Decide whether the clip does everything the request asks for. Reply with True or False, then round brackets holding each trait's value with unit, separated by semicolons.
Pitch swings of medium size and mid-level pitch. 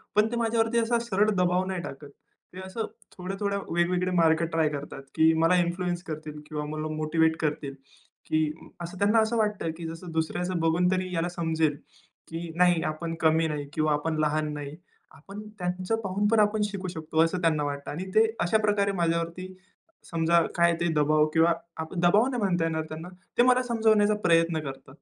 True (3.6 semitones; 170 Hz)